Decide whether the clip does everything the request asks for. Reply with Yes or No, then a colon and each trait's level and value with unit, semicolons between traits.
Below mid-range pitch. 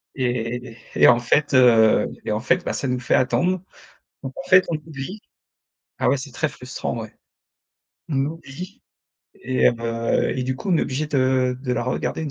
Yes: low, 130 Hz